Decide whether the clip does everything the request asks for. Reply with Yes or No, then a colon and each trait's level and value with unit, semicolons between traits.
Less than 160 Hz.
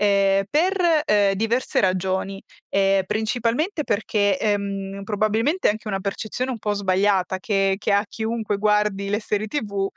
No: high, 205 Hz